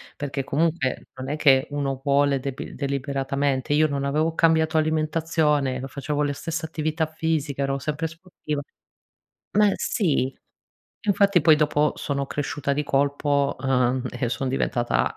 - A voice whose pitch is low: No, medium, 145 Hz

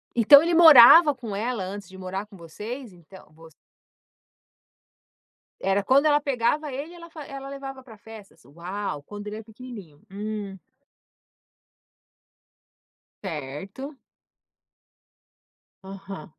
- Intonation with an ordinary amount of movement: No, wide, 6.1 semitones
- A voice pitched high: Yes, high, 215 Hz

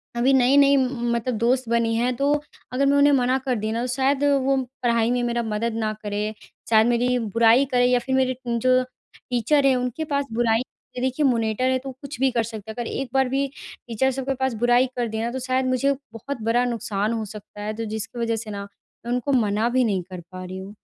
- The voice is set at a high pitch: Yes, high, 245 Hz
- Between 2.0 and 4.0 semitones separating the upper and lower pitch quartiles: Yes, narrow, 2.6 semitones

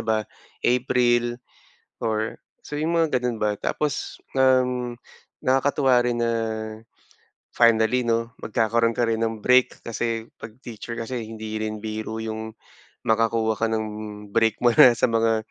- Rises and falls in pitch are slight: Yes, narrow, 1.8 semitones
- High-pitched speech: No, low, 115 Hz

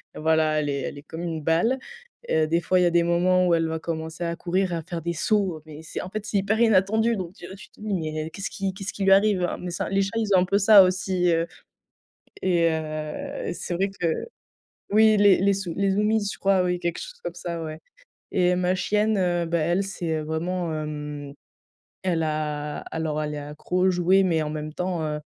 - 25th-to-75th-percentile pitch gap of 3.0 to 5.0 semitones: Yes, average, 3.3 semitones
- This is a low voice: No, medium, 175 Hz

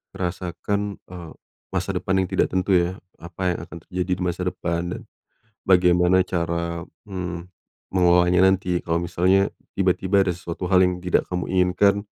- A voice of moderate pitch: No, very low, 90 Hz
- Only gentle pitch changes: Yes, narrow, 1.2 semitones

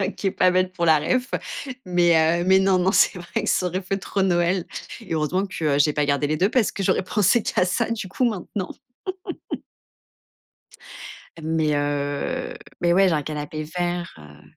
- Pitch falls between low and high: Yes, medium, 175 Hz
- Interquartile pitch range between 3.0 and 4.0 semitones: Yes, average, 3.6 semitones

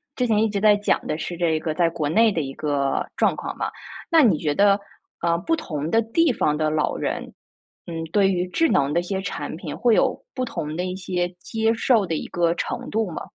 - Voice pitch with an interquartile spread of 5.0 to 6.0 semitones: Yes, wide, 5.5 semitones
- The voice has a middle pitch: Yes, medium, 180 Hz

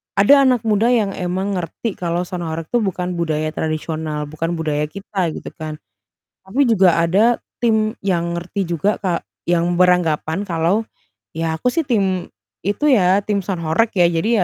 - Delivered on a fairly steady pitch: No, average, 3.8 semitones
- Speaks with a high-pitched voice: No, medium, 180 Hz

